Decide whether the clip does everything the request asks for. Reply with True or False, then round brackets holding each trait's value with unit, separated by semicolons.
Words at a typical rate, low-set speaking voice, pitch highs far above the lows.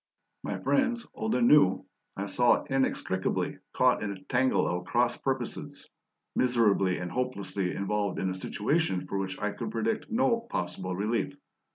True (155 wpm; 105 Hz; 6.2 semitones)